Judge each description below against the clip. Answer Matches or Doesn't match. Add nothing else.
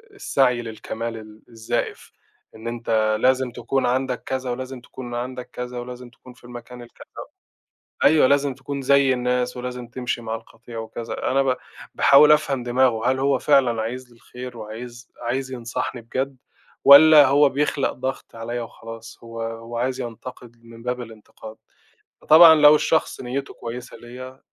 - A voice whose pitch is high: Doesn't match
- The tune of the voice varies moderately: Doesn't match